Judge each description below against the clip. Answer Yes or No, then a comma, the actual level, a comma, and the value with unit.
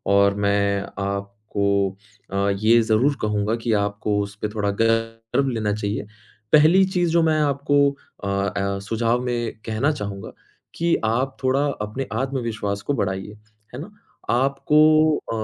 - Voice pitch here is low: Yes, low, 115 Hz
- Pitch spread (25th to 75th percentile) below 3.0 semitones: No, average, 5.1 semitones